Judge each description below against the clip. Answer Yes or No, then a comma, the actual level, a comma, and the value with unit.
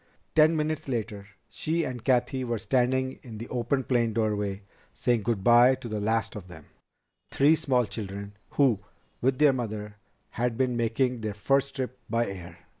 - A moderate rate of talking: Yes, average, 170 wpm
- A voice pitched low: Yes, low, 120 Hz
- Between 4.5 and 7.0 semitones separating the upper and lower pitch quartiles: No, average, 3.6 semitones